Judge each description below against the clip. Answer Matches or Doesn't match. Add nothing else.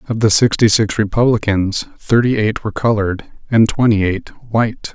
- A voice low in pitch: Matches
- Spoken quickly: Doesn't match